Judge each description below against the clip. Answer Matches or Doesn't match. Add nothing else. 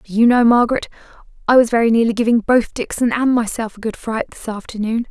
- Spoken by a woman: Matches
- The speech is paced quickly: Matches